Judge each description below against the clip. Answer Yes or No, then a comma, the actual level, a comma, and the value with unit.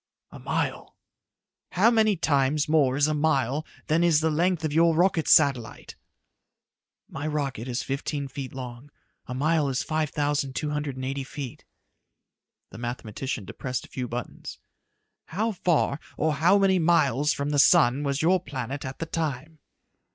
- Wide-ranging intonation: No, average, 3.2 semitones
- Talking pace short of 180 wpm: Yes, average, 160 wpm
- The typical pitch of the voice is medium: Yes, medium, 145 Hz